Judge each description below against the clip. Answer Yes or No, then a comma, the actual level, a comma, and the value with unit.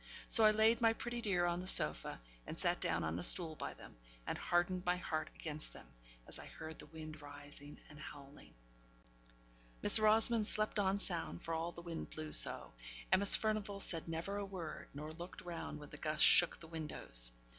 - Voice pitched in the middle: Yes, medium, 170 Hz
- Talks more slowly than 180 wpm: No, average, 195 wpm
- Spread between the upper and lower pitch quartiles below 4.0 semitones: No, average, 4.5 semitones